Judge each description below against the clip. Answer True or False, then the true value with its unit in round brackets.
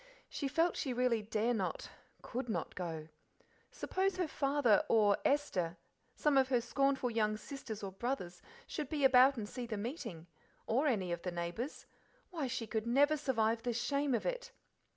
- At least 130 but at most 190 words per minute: True (170 wpm)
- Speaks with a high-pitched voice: True (245 Hz)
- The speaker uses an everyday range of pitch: True (4.6 semitones)